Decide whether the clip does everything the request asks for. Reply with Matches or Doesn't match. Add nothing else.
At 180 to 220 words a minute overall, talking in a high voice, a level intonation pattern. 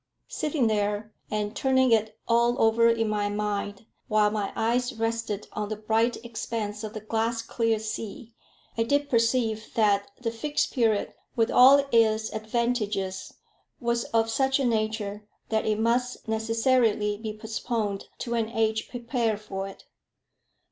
Doesn't match